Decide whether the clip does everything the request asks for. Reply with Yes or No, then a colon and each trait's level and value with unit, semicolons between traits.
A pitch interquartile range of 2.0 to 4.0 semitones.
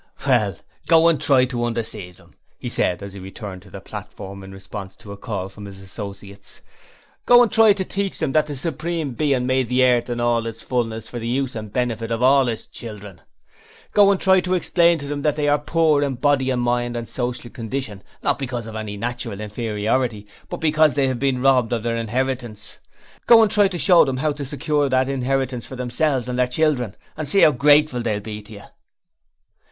No: average, 4.7 semitones